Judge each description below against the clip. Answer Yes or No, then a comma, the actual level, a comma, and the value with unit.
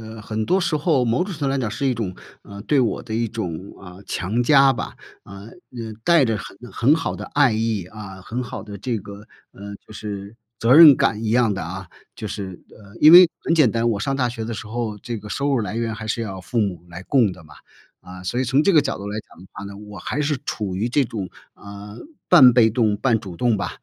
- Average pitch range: Yes, average, 3.9 semitones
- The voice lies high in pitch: No, low, 110 Hz